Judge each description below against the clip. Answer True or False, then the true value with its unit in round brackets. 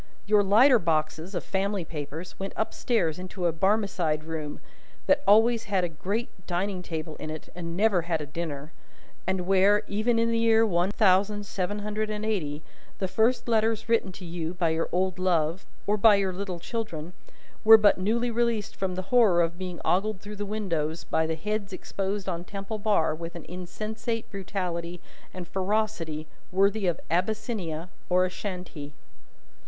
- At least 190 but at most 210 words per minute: False (170 wpm)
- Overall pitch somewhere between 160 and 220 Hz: True (190 Hz)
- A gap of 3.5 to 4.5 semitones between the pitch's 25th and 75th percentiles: True (3.9 semitones)